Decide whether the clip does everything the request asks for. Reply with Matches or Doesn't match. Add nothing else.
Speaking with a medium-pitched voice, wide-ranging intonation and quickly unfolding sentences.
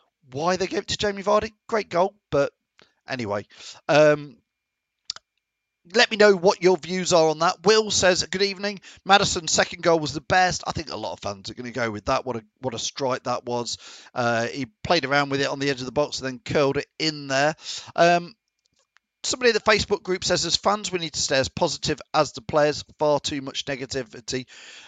Matches